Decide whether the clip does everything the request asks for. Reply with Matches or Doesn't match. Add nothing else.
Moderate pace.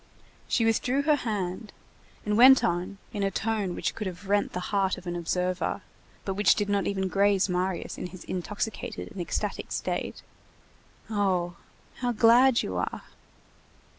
Matches